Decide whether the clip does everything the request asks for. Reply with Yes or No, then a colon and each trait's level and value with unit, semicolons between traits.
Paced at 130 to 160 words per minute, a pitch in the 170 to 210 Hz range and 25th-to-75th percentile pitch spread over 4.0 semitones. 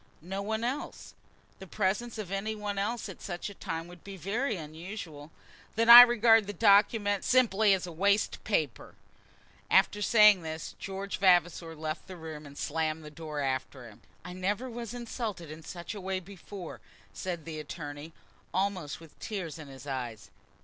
No: average, 170 wpm; medium, 185 Hz; average, 4.7 semitones